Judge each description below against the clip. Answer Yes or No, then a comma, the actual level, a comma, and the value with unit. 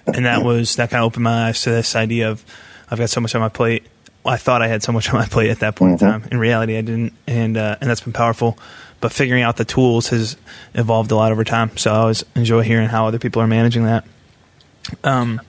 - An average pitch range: No, narrow, 1.0 semitones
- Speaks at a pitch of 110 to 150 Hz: Yes, low, 115 Hz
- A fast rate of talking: Yes, fast, 260 wpm